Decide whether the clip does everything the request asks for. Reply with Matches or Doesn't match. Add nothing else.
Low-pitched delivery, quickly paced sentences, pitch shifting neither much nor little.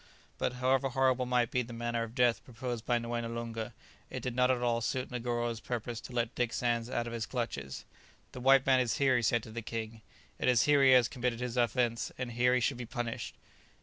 Doesn't match